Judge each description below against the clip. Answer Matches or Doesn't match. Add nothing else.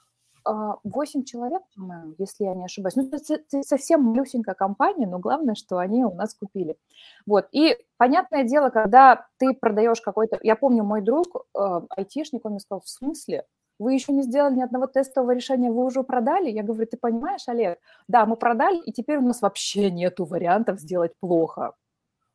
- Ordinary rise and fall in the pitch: Matches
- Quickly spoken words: Matches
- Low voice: Doesn't match